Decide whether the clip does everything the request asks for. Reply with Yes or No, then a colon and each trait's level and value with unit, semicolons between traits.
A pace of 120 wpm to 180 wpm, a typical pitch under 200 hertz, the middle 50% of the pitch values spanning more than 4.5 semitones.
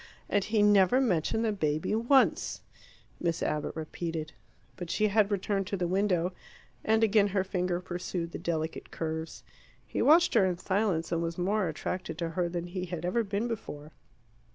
No: average, 175 wpm; medium, 185 Hz; average, 3.6 semitones